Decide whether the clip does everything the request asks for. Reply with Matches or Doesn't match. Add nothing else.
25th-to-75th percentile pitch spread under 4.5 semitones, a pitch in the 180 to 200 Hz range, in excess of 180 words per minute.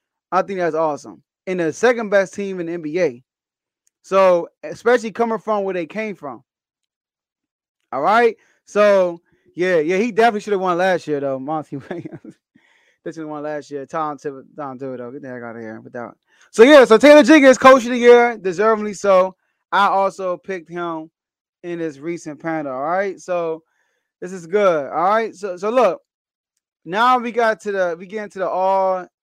Doesn't match